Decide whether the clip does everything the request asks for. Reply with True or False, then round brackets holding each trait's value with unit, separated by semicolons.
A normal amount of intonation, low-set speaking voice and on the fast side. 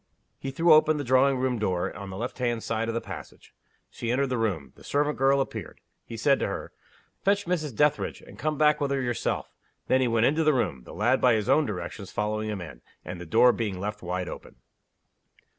True (4.9 semitones; 120 Hz; 225 wpm)